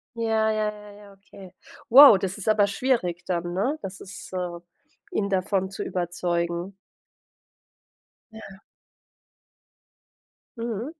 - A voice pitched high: Yes, high, 195 Hz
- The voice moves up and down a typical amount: Yes, average, 3.1 semitones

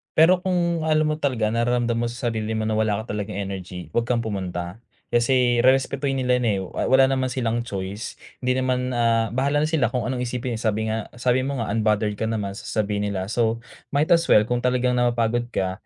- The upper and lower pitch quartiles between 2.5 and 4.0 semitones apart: Yes, average, 2.9 semitones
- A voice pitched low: Yes, low, 120 Hz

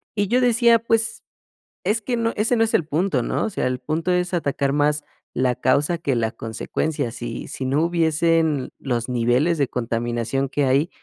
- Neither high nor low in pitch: Yes, medium, 150 Hz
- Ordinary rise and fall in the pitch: No, wide, 6.1 semitones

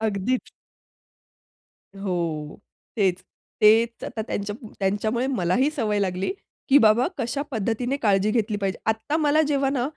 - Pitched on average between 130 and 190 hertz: No, high, 220 Hz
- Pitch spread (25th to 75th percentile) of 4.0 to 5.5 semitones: Yes, average, 4.3 semitones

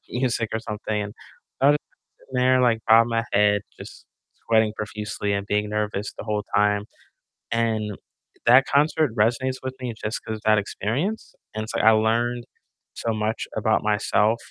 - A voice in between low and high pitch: No, low, 110 Hz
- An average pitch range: No, narrow, 2.1 semitones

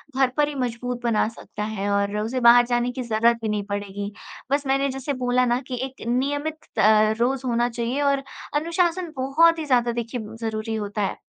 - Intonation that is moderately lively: Yes, average, 3.7 semitones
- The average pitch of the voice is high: Yes, high, 245 Hz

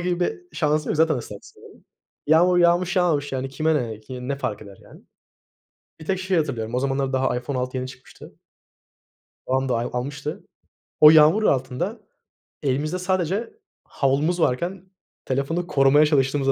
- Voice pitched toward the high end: No, medium, 145 Hz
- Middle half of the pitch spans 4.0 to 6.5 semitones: Yes, average, 4.8 semitones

